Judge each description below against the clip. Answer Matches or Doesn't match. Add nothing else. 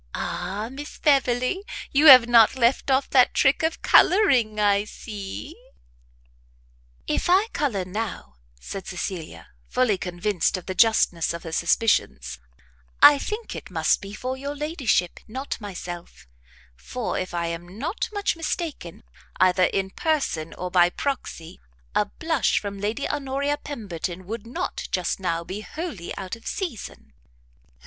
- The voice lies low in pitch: Doesn't match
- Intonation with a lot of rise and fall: Matches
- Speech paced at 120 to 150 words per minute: Matches